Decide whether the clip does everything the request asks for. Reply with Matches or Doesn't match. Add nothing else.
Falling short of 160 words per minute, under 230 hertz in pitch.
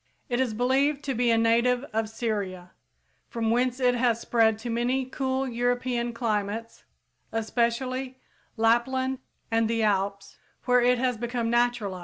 Doesn't match